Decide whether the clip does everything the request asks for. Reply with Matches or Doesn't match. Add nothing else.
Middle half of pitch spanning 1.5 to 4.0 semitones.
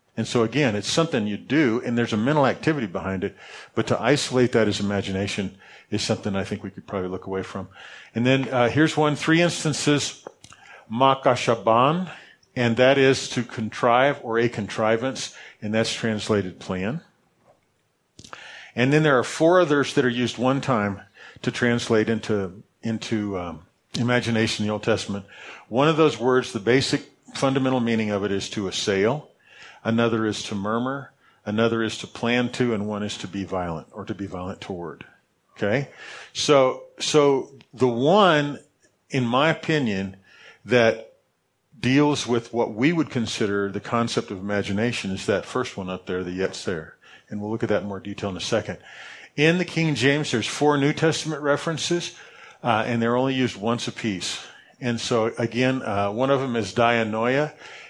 Doesn't match